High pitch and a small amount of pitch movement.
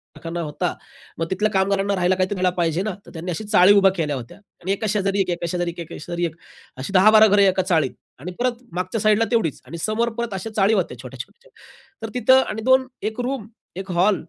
No: high, 195 Hz; average, 3.7 semitones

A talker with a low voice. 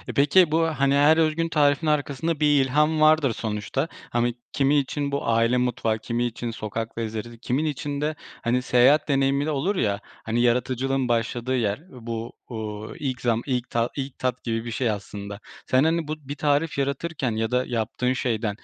Yes: low, 130 Hz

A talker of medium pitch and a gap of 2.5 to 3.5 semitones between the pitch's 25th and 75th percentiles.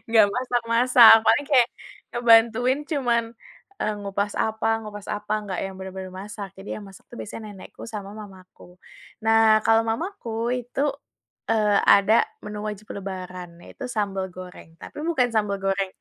No: high, 215 Hz; average, 3.0 semitones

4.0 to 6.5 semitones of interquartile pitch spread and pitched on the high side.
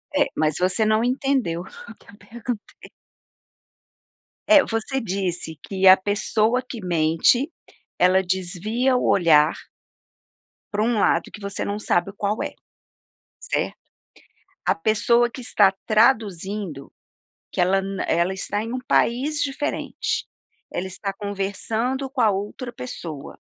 Yes: average, 4.3 semitones; high, 205 Hz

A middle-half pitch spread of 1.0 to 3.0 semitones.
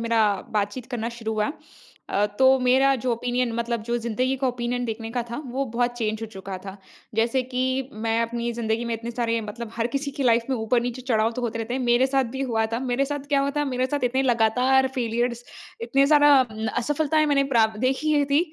Yes: narrow, 2.5 semitones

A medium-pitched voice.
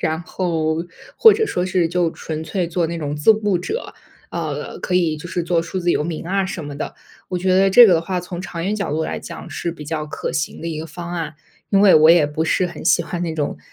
Yes: medium, 170 Hz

